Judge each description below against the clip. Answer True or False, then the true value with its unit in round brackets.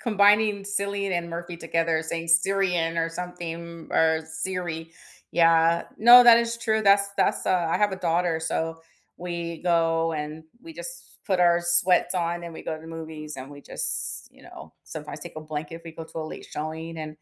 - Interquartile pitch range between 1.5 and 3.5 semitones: True (2.6 semitones)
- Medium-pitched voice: True (170 Hz)